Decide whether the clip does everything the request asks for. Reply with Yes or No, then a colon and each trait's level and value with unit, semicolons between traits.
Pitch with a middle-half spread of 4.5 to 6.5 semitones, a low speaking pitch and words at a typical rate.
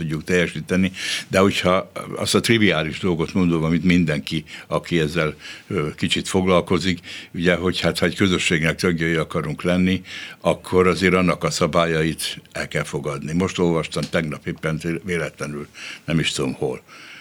No: narrow, 2.4 semitones; very low, 85 Hz; average, 140 wpm